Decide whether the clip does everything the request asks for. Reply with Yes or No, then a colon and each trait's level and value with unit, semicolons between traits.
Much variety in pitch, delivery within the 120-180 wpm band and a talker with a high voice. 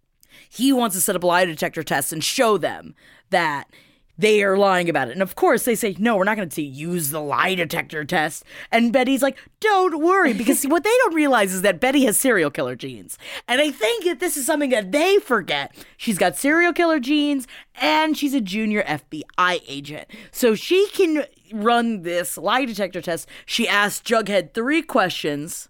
No: wide, 8.4 semitones; average, 195 wpm; high, 225 Hz